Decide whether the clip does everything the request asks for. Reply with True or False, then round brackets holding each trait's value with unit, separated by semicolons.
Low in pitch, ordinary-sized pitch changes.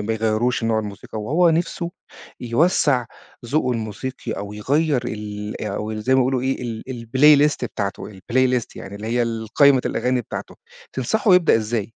True (120 Hz; 3.6 semitones)